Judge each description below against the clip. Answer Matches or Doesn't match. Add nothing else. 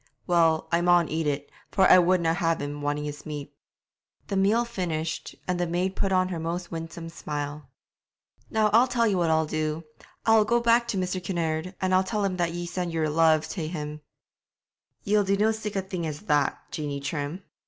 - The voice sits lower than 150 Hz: Doesn't match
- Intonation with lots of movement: Doesn't match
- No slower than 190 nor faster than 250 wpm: Matches